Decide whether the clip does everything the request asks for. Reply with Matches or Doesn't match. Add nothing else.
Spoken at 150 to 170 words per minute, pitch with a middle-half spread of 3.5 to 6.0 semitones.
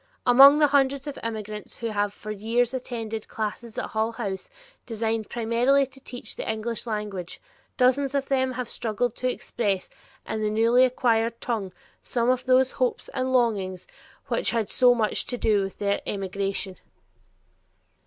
Doesn't match